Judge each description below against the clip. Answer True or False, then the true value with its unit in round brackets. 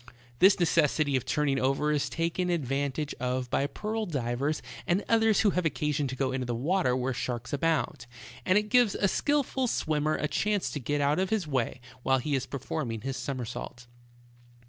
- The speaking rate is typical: True (185 wpm)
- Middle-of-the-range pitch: True (145 Hz)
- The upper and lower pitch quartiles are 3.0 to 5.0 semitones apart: False (5.6 semitones)